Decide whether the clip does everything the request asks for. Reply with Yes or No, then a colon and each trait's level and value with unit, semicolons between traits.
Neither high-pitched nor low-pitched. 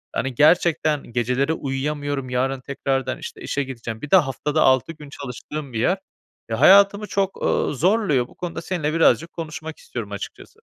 Yes: medium, 145 Hz